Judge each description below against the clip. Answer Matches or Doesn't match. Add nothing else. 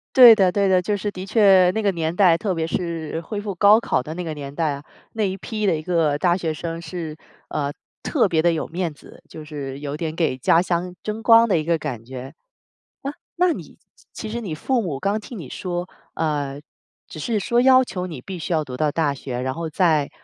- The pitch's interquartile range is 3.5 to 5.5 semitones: Matches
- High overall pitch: Doesn't match